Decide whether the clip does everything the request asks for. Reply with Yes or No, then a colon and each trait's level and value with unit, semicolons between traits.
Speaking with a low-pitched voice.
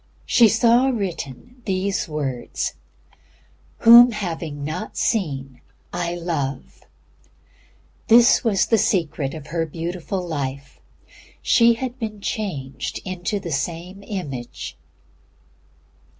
No: medium, 175 Hz